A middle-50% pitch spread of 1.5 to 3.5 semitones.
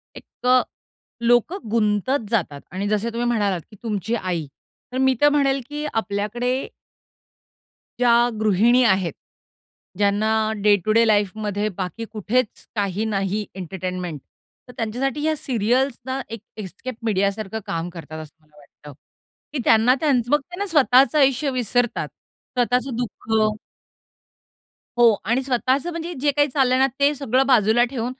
No: average, 4.2 semitones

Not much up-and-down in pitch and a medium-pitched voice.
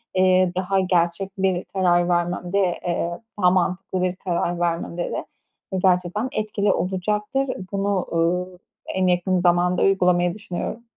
Yes: narrow, 1.6 semitones; medium, 180 Hz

